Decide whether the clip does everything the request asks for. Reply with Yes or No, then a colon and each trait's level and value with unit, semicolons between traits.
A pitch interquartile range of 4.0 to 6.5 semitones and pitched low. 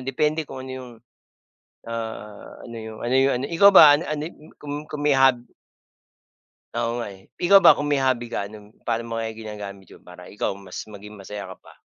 Yes: wide, 5.5 semitones; low, 120 Hz